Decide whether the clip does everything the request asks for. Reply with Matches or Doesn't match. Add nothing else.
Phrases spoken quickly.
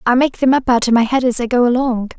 Matches